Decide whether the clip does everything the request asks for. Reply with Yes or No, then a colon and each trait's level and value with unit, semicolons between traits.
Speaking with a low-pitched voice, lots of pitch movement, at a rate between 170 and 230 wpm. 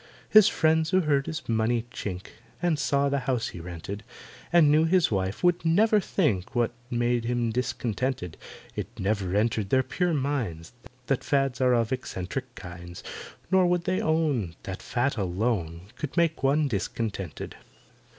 No: low, 125 Hz; wide, 7.4 semitones; average, 155 wpm